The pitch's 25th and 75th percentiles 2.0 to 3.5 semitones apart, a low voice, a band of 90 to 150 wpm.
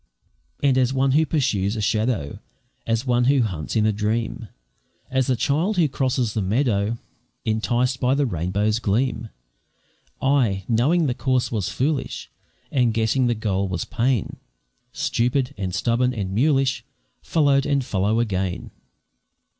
No: average, 4.0 semitones; low, 120 Hz; average, 145 wpm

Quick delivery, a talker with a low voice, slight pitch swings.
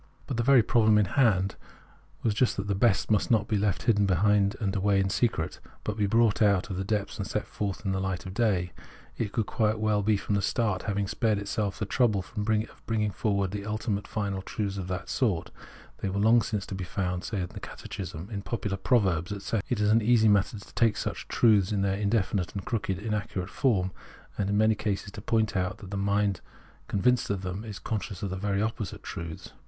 Yes: fast, 220 wpm; low, 100 Hz; narrow, 2.2 semitones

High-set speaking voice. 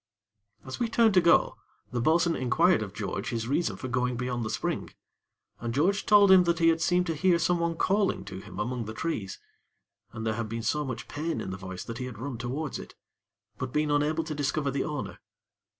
No: medium, 140 Hz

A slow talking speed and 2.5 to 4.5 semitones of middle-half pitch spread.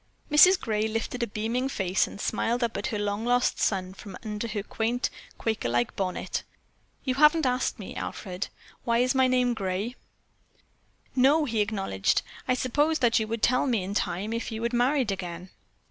No: average, 180 wpm; average, 3.8 semitones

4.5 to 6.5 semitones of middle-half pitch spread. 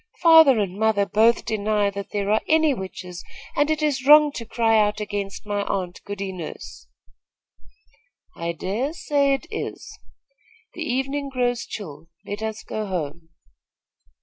Yes: wide, 5.5 semitones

